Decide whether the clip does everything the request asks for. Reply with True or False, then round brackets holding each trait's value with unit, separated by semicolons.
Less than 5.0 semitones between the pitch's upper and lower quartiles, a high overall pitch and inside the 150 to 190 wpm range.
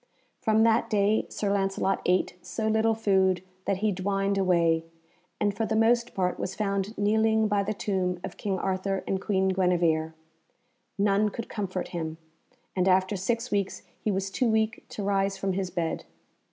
True (2.4 semitones; 195 Hz; 170 wpm)